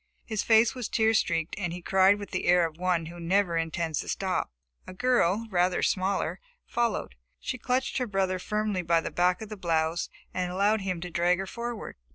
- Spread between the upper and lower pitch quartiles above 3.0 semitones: Yes, average, 3.7 semitones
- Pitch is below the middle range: No, medium, 185 Hz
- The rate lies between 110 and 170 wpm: No, fast, 205 wpm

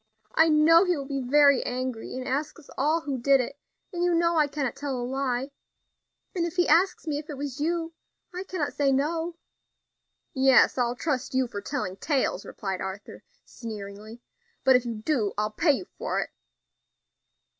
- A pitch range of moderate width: Yes, average, 4.5 semitones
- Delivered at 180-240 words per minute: Yes, average, 185 wpm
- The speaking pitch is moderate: No, very high, 275 Hz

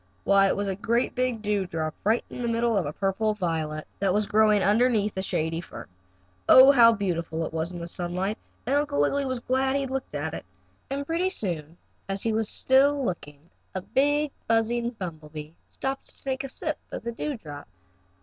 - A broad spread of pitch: Yes, wide, 6.6 semitones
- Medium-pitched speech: No, high, 210 Hz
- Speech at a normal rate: No, fast, 210 wpm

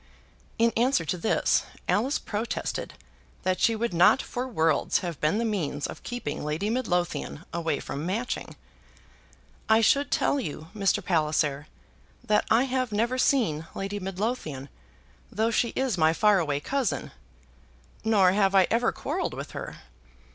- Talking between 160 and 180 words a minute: No, average, 145 wpm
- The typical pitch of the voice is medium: No, high, 200 Hz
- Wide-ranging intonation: Yes, wide, 6.2 semitones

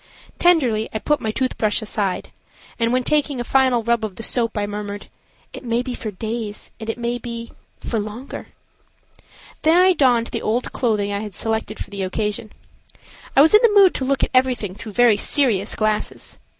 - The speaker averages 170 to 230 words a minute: Yes, average, 190 wpm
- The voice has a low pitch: No, high, 230 Hz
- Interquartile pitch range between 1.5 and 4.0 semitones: Yes, average, 3.3 semitones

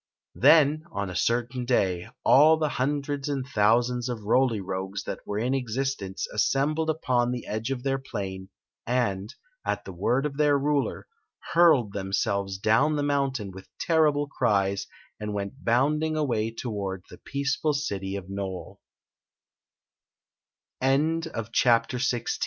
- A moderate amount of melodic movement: No, wide, 5.8 semitones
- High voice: No, low, 125 Hz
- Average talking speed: Yes, average, 145 wpm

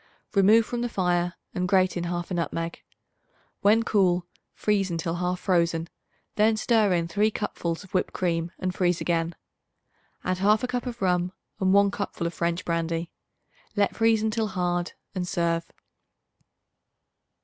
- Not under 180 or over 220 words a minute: No, average, 150 wpm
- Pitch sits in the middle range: Yes, medium, 180 Hz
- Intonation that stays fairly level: No, average, 3.2 semitones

